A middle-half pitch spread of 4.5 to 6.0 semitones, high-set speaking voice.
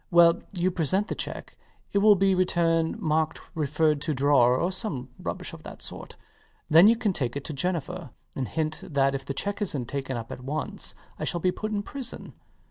No: average, 4.9 semitones; medium, 160 Hz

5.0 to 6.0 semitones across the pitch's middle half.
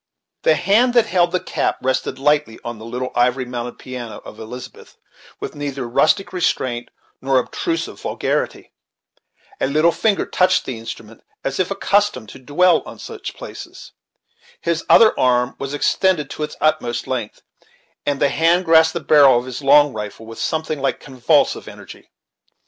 Yes: average, 5.3 semitones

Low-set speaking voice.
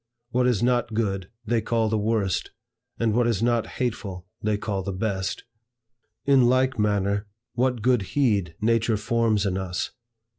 Yes: low, 110 Hz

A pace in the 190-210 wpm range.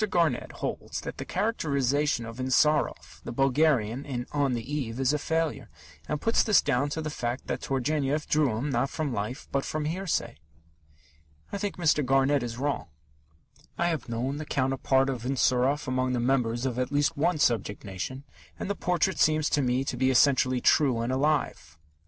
No: average, 180 wpm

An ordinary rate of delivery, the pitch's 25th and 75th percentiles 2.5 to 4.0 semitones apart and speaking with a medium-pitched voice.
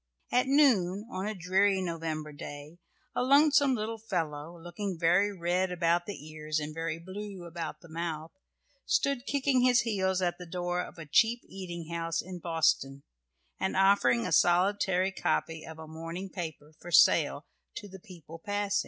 Yes: average, 165 wpm; average, 3.7 semitones; medium, 180 Hz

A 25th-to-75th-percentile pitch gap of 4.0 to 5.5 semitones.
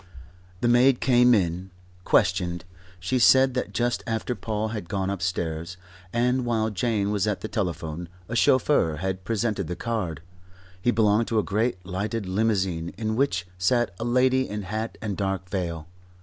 Yes: average, 4.4 semitones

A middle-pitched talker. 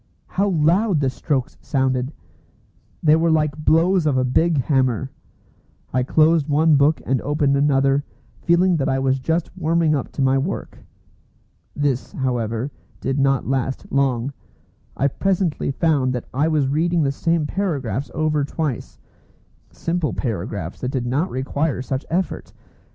Yes: medium, 145 Hz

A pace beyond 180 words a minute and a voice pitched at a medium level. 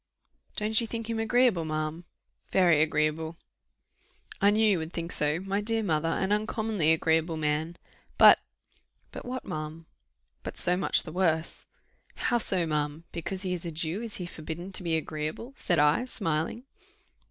No: average, 165 wpm; medium, 170 Hz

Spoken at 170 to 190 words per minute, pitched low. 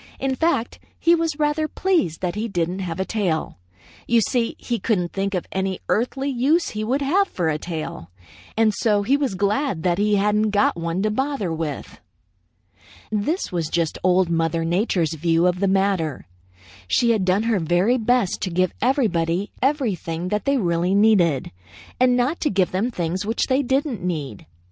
No: average, 180 wpm; high, 200 Hz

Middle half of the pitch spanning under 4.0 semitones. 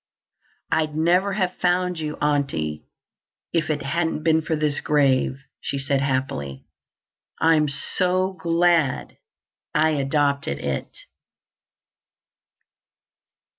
Yes: average, 3.4 semitones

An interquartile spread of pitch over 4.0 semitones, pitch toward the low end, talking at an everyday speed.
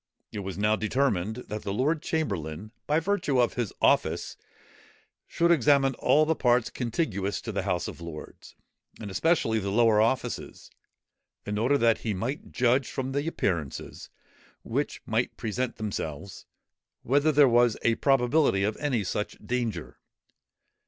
Yes: average, 5.1 semitones; low, 120 Hz; average, 145 wpm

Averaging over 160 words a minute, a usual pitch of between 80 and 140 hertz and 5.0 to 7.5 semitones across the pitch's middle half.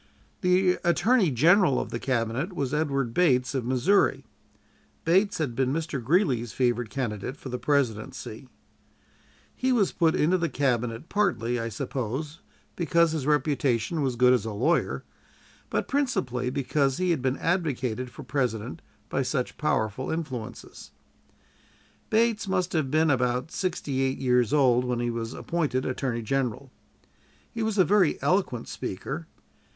No: average, 145 wpm; low, 135 Hz; average, 5.3 semitones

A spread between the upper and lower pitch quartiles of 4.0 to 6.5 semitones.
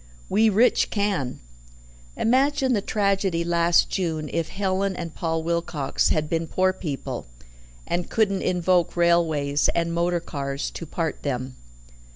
No: average, 3.2 semitones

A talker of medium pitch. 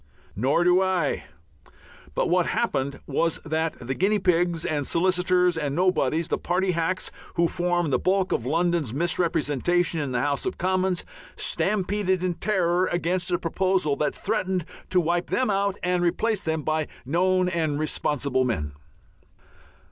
Yes: medium, 175 Hz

